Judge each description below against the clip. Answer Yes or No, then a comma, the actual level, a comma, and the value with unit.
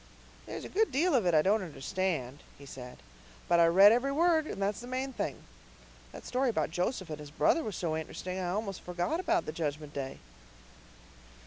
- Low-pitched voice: No, medium, 185 Hz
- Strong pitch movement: Yes, wide, 8.3 semitones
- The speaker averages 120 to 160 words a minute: No, average, 200 wpm